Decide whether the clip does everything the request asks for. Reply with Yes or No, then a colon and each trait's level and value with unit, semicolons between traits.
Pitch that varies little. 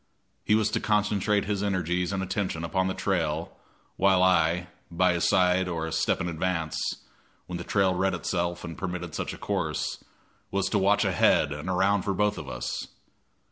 Yes: narrow, 2.3 semitones